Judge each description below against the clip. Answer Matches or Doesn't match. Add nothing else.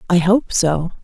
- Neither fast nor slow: Matches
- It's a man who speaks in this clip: Doesn't match